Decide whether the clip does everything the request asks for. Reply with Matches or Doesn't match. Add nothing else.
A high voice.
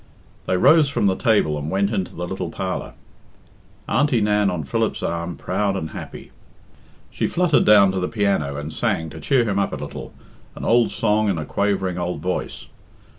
Doesn't match